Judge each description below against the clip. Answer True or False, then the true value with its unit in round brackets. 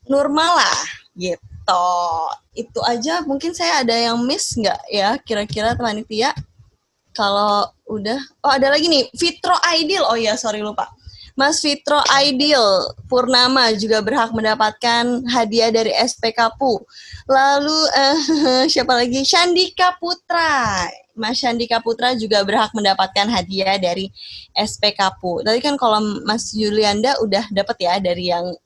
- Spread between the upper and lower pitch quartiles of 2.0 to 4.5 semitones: False (4.9 semitones)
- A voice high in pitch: True (235 Hz)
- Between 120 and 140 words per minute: True (135 wpm)